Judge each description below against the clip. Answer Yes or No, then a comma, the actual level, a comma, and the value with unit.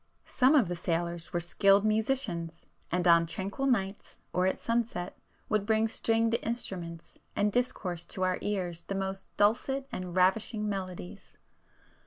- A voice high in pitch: Yes, high, 195 Hz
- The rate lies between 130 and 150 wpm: Yes, average, 145 wpm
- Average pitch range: Yes, average, 4.0 semitones